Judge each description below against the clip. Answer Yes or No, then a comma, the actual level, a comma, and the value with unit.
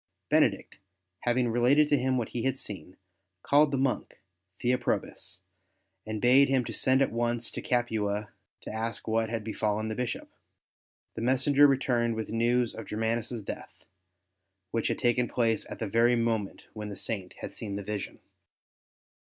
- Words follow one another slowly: No, average, 160 wpm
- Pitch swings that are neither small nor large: No, narrow, 2.3 semitones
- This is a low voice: Yes, low, 115 Hz